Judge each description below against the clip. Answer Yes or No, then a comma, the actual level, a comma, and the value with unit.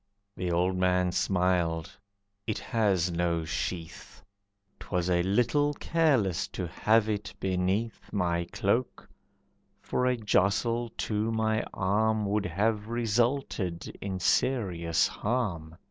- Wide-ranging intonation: No, average, 4.0 semitones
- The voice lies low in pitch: Yes, low, 100 Hz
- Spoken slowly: Yes, slow, 115 wpm